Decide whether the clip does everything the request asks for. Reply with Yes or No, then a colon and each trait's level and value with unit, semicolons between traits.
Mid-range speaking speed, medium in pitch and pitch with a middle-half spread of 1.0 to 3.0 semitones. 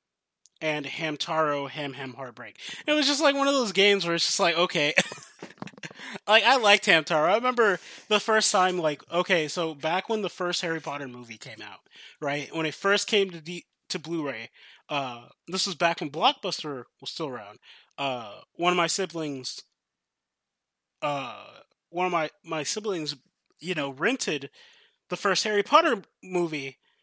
No: average, 170 wpm; medium, 175 Hz; average, 5.2 semitones